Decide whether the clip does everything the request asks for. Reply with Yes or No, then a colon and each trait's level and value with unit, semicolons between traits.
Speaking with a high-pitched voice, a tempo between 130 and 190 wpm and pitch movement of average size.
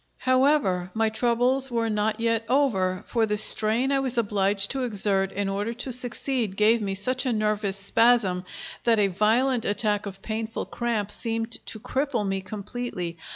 Yes: high, 220 Hz; average, 165 wpm; average, 3.4 semitones